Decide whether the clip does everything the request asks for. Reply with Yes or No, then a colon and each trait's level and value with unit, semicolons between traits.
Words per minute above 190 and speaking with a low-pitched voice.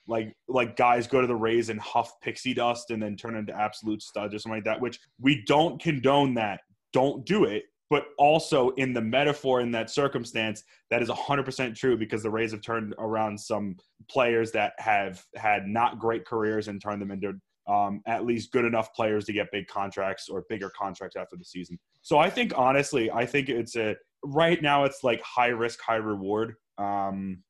Yes: fast, 205 wpm; low, 115 Hz